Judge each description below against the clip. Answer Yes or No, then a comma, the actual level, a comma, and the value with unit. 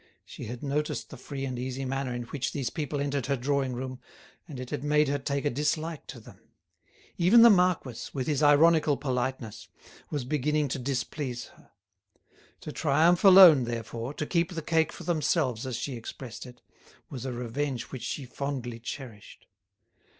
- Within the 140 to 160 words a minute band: No, average, 175 wpm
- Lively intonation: No, average, 3.3 semitones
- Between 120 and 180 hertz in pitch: Yes, medium, 140 Hz